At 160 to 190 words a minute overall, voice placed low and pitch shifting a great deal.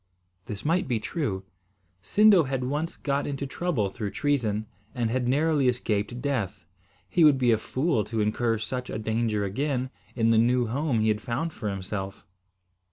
No: average, 170 wpm; low, 120 Hz; average, 4.6 semitones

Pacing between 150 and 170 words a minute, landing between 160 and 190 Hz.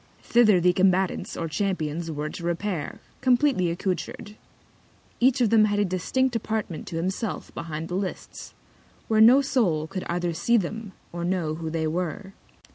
Yes: average, 160 wpm; medium, 185 Hz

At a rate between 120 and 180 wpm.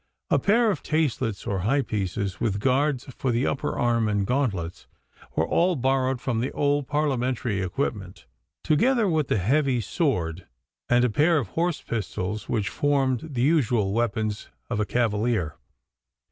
Yes: average, 155 wpm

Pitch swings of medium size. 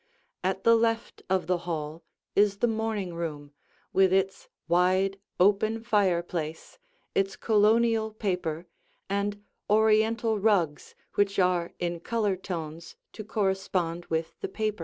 Yes: average, 3.8 semitones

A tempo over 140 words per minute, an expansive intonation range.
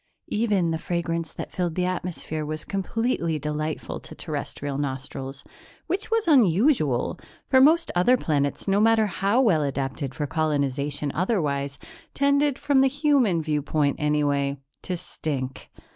No: slow, 135 wpm; wide, 7.6 semitones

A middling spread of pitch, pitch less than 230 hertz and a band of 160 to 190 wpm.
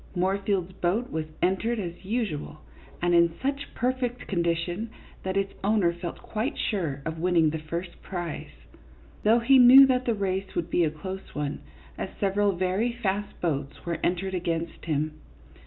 Yes: average, 4.1 semitones; medium, 185 Hz; average, 165 wpm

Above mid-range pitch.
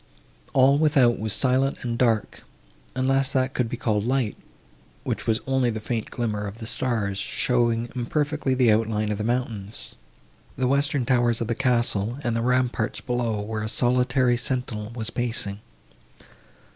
No: low, 120 Hz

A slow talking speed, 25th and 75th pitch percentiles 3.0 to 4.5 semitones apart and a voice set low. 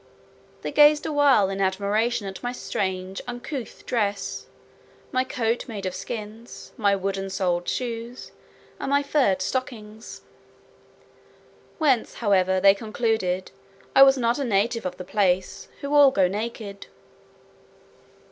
No: slow, 130 wpm; average, 4.2 semitones; high, 215 Hz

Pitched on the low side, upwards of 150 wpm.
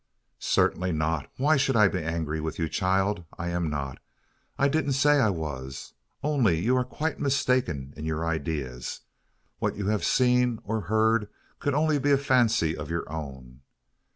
Yes: very low, 95 Hz; average, 160 wpm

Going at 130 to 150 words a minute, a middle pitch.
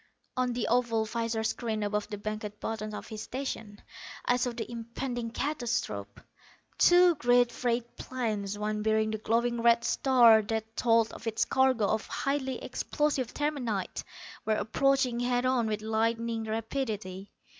No: average, 145 wpm; high, 230 Hz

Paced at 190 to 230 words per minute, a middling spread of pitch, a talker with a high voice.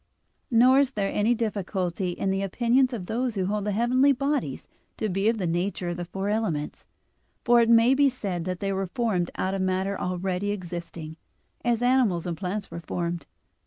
Yes: average, 195 wpm; average, 4.6 semitones; high, 200 Hz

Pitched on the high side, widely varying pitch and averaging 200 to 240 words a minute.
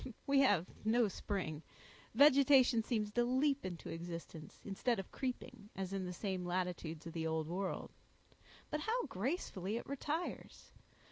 No: high, 205 Hz; wide, 6.6 semitones; average, 145 wpm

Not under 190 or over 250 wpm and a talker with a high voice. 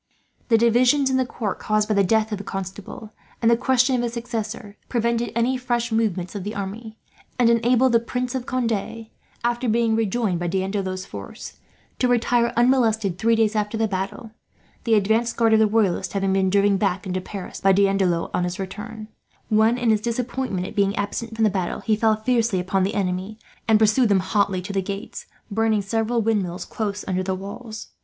Yes: average, 195 wpm; high, 220 Hz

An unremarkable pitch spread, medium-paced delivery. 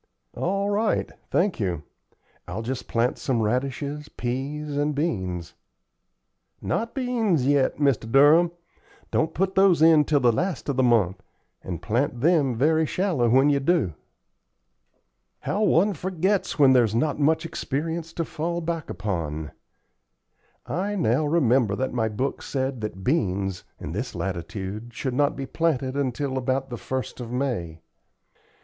No: wide, 5.8 semitones; average, 145 wpm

